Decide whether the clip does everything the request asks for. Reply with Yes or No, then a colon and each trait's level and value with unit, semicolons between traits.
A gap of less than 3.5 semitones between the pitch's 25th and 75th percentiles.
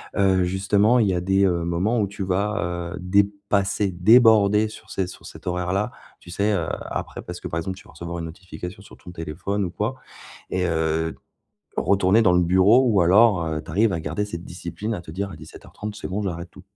Yes: average, 2.9 semitones